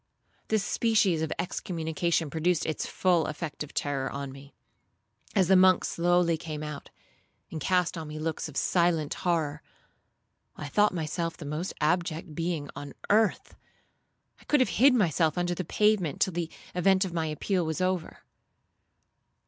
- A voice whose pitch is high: No, medium, 170 Hz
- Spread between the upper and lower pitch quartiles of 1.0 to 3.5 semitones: Yes, average, 3.1 semitones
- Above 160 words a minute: No, average, 155 wpm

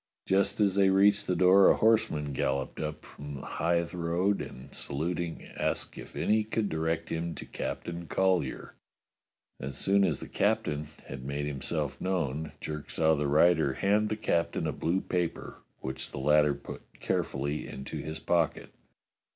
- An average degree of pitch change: Yes, average, 4.6 semitones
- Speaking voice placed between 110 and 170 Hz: No, very low, 80 Hz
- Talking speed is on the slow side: No, average, 160 wpm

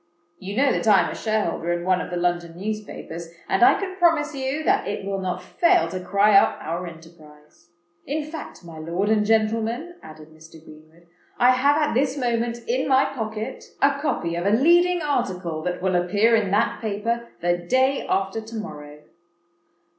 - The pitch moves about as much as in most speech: No, wide, 7.0 semitones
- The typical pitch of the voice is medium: No, high, 210 Hz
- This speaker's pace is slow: No, average, 185 wpm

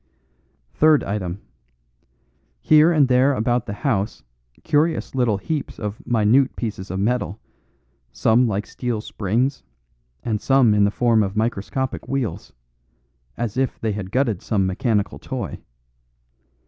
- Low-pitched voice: Yes, low, 115 Hz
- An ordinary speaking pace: No, slow, 130 wpm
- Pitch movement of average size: Yes, average, 4.3 semitones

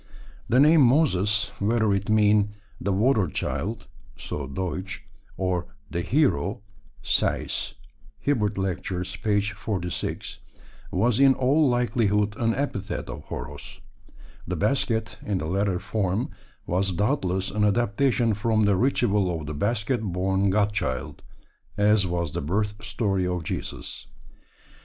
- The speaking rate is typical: No, slow, 130 wpm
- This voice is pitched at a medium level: No, low, 105 Hz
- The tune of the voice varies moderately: Yes, average, 3.3 semitones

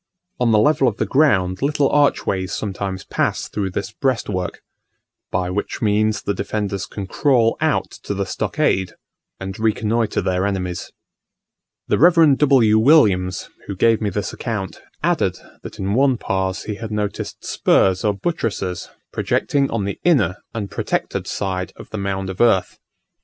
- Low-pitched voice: Yes, low, 105 Hz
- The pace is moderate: Yes, average, 155 wpm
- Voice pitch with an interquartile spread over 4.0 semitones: No, average, 3.6 semitones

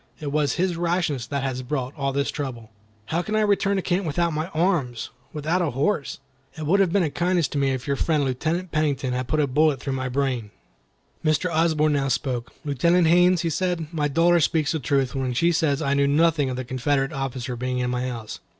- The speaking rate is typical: No, fast, 220 wpm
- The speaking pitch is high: No, medium, 145 Hz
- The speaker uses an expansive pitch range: No, average, 4.2 semitones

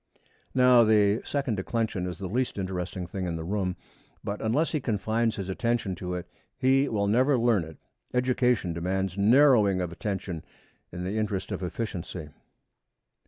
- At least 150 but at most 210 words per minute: Yes, average, 160 wpm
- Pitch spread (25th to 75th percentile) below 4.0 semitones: No, average, 4.5 semitones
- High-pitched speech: No, low, 100 Hz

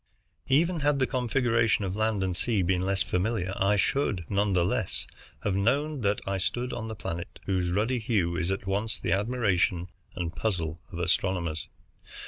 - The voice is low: Yes, low, 100 Hz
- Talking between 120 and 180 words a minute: Yes, average, 175 wpm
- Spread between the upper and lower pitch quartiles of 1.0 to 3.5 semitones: No, average, 4.0 semitones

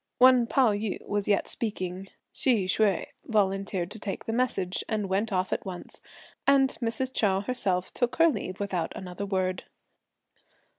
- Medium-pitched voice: No, high, 205 Hz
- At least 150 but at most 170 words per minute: Yes, average, 155 wpm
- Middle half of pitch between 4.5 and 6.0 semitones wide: No, average, 3.7 semitones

